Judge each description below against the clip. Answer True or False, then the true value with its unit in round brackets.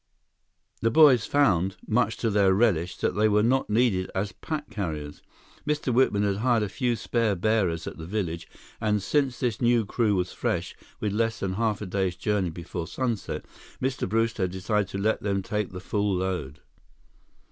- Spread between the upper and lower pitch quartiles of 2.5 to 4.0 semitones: True (3.6 semitones)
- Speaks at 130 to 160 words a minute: False (180 wpm)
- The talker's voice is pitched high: False (105 Hz)